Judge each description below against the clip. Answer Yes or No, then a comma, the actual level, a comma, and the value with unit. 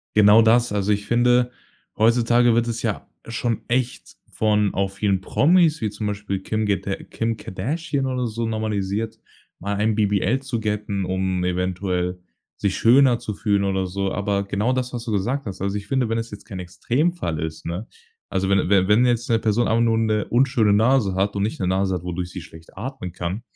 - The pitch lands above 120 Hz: No, low, 105 Hz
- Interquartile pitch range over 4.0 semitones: No, average, 3.4 semitones